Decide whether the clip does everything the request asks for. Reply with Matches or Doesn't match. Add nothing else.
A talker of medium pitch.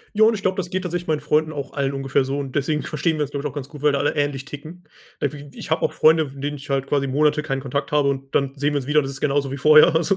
Matches